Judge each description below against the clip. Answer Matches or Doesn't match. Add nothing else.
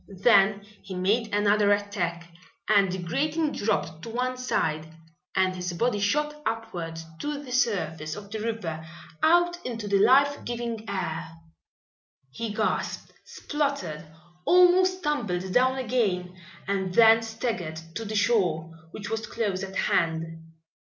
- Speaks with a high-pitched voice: Matches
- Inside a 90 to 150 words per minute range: Matches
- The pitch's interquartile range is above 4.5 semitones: Matches